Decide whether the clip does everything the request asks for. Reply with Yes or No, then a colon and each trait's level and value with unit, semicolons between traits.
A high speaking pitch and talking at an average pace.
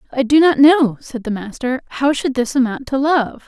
No: very high, 265 Hz; fast, 225 wpm